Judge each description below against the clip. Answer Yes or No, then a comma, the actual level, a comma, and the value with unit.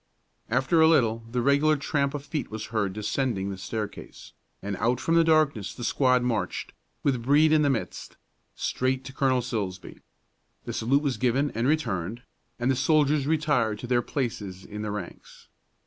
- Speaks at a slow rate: No, average, 175 wpm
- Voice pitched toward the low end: Yes, low, 125 Hz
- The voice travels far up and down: No, average, 4.4 semitones